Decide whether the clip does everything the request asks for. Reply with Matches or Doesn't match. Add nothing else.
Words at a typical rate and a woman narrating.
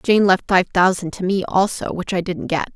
Doesn't match